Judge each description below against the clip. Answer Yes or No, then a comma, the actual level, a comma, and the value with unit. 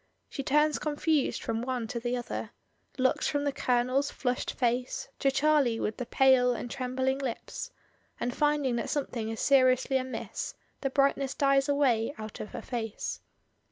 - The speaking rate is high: No, average, 160 wpm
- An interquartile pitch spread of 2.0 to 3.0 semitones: Yes, narrow, 2.4 semitones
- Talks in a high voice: Yes, very high, 260 Hz